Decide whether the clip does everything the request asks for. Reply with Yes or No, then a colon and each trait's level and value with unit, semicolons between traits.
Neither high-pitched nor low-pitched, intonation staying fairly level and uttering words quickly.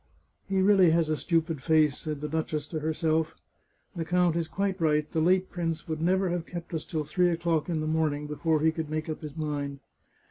Yes: medium, 160 Hz; narrow, 2.0 semitones; fast, 225 wpm